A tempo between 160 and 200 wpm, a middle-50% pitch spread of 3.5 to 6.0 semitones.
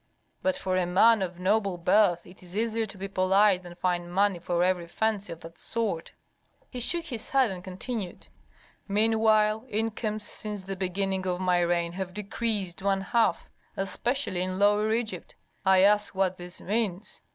No: average, 170 wpm; average, 3.0 semitones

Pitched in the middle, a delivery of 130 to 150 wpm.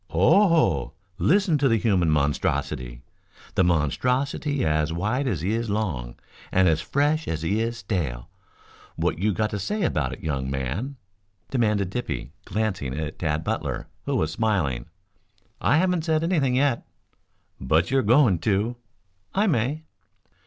No: low, 105 Hz; average, 145 wpm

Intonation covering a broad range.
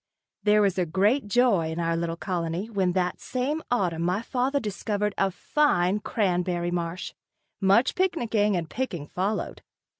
No: average, 4.6 semitones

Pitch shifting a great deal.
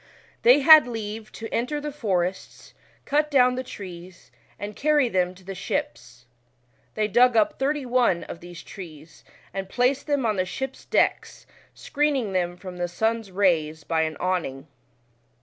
Yes: wide, 6.2 semitones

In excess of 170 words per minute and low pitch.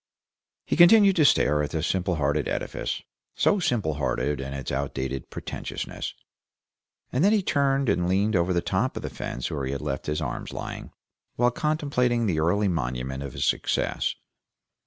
Yes: average, 180 wpm; very low, 85 Hz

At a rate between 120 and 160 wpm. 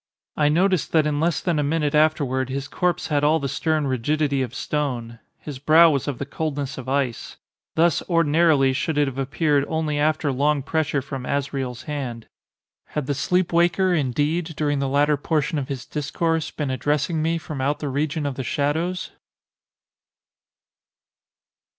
No: average, 170 wpm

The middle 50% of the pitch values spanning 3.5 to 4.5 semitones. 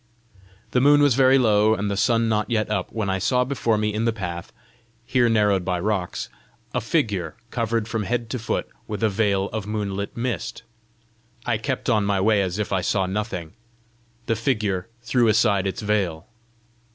No: average, 2.8 semitones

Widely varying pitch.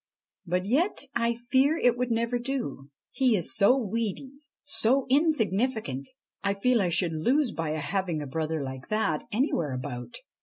Yes: wide, 7.7 semitones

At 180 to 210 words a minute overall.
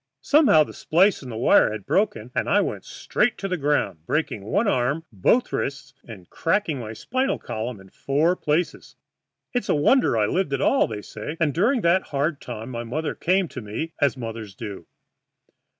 Yes: average, 190 wpm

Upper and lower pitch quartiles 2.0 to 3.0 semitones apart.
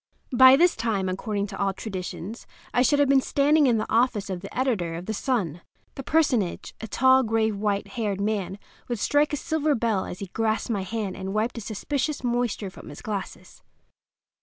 No: average, 4.7 semitones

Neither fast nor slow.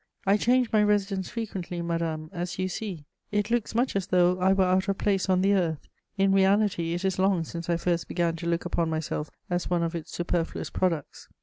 No: fast, 215 wpm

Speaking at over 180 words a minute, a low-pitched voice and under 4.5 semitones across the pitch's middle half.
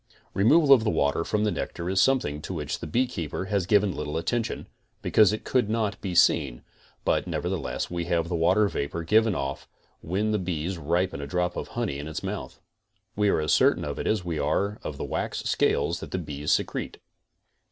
No: fast, 205 wpm; very low, 90 Hz; wide, 5.4 semitones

